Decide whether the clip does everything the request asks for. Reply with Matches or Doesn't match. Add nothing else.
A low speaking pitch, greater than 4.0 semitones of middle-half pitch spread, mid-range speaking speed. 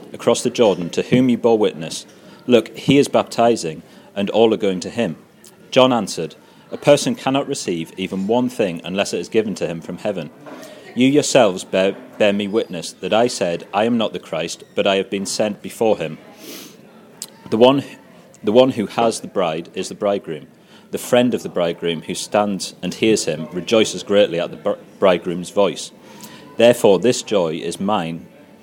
Matches